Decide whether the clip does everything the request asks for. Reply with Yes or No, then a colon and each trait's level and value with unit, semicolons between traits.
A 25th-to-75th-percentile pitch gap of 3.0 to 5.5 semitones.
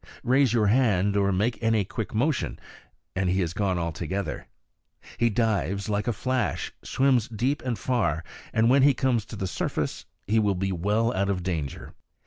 Yes: average, 4.0 semitones